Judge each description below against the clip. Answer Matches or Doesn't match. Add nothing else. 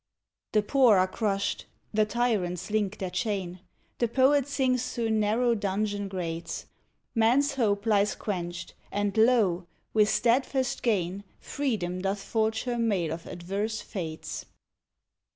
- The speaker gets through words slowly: Matches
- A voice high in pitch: Matches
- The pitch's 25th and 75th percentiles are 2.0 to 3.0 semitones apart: Doesn't match